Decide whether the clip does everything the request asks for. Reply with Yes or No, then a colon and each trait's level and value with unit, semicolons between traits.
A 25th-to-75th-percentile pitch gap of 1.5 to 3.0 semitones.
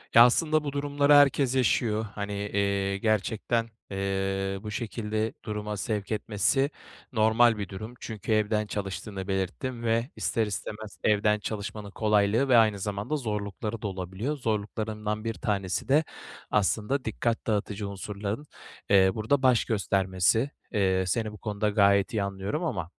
Yes: narrow, 2.5 semitones